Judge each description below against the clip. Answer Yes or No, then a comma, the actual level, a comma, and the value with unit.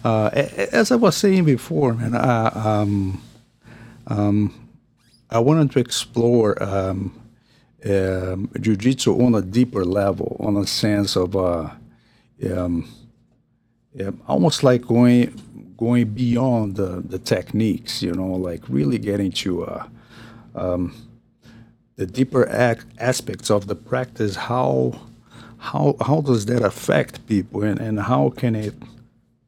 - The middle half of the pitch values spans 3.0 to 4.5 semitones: Yes, average, 3.5 semitones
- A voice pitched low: Yes, low, 115 Hz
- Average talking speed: No, slow, 130 wpm